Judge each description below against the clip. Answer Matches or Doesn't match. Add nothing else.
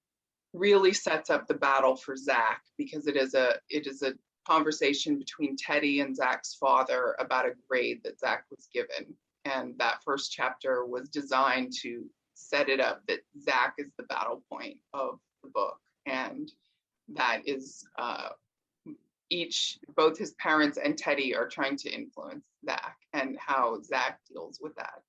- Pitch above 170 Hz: Matches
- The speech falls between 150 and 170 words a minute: Matches